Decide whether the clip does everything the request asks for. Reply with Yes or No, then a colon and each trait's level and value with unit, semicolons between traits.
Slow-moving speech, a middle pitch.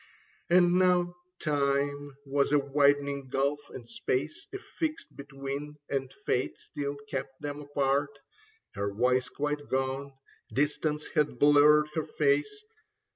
Yes: slow, 125 wpm; medium, 145 Hz